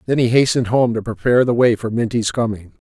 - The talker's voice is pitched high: No, low, 115 Hz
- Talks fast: Yes, fast, 230 wpm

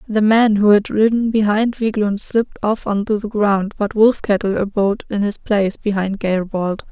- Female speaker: Yes, female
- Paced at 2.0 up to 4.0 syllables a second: No, 4.8 syllables/s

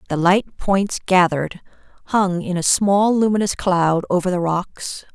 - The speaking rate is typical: Yes, average, 150 wpm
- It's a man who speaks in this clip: No, female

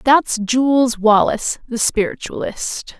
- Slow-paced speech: Yes, slow, 100 wpm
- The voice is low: No, high, 235 Hz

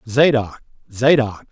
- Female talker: No, male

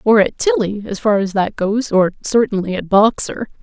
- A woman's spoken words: Yes, female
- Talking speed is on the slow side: No, average, 200 wpm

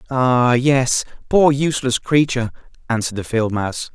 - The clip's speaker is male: Yes, male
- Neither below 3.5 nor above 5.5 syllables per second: Yes, 5.1 syllables/s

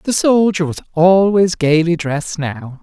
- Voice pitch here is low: No, medium, 170 Hz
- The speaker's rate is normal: Yes, average, 150 wpm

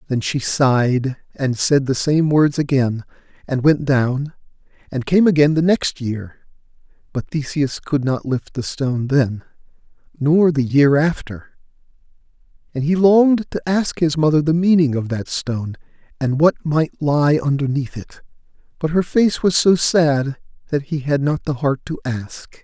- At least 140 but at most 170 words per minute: Yes, average, 165 wpm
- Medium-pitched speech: Yes, medium, 145 Hz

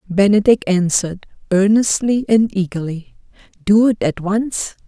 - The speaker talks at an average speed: No, slow, 110 wpm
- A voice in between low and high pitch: No, high, 200 Hz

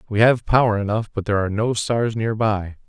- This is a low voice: Yes, low, 110 Hz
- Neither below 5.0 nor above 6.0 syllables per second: Yes, 5.8 syllables/s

